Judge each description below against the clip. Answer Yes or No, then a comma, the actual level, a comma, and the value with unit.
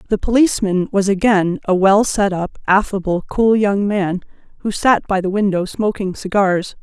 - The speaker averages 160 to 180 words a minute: Yes, average, 165 wpm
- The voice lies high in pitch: Yes, high, 200 Hz